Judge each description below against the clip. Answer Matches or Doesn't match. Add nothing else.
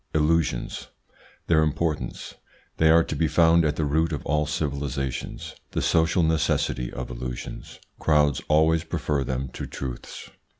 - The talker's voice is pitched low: Matches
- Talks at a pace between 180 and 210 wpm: Doesn't match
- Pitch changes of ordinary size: Matches